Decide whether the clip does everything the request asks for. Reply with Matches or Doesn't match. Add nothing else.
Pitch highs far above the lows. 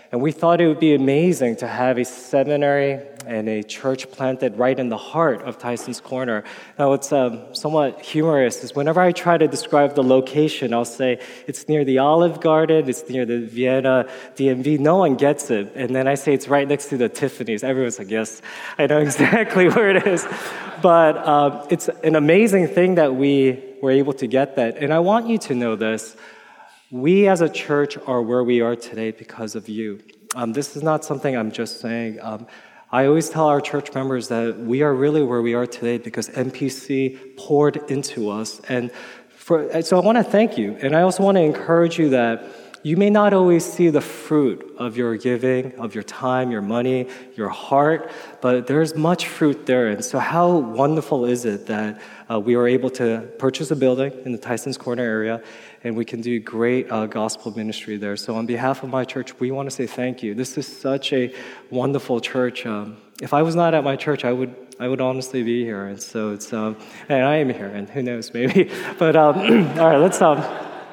Doesn't match